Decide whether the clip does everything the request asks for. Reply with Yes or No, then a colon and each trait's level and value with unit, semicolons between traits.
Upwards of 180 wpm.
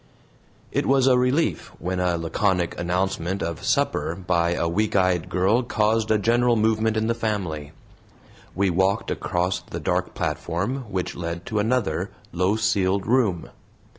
No: average, 150 wpm